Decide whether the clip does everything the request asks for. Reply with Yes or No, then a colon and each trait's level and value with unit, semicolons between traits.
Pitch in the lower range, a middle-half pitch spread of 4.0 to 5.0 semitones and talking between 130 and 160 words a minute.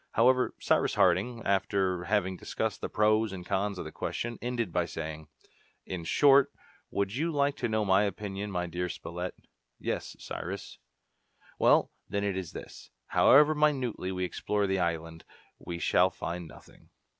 Yes: very low, 95 Hz; average, 4.3 semitones; average, 155 wpm